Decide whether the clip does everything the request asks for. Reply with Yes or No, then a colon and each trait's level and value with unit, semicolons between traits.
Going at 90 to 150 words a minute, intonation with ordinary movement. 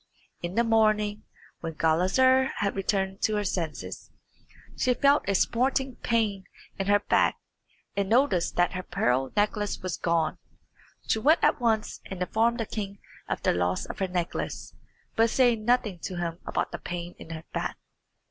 No: average, 165 wpm; average, 4.4 semitones